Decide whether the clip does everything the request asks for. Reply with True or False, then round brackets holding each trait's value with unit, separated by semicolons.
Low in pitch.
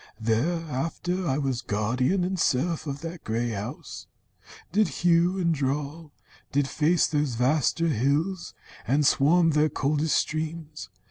False (150 Hz)